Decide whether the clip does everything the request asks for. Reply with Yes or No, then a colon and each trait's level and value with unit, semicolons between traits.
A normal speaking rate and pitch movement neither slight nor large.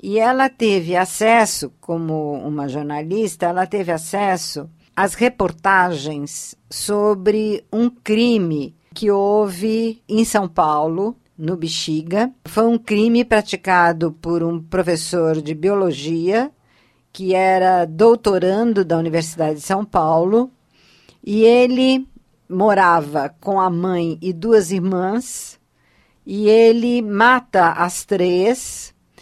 No: slow, 110 wpm; average, 4.7 semitones